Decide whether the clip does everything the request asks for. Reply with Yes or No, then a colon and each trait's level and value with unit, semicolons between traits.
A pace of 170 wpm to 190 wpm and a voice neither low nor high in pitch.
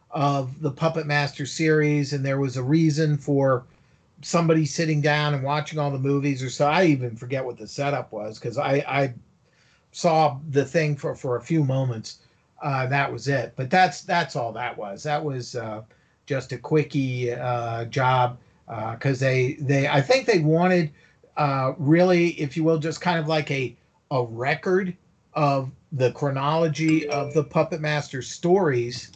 Yes: average, 175 wpm; medium, 145 Hz